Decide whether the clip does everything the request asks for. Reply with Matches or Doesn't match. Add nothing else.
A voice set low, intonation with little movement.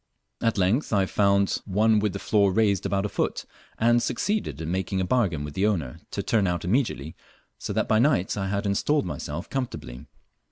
Doesn't match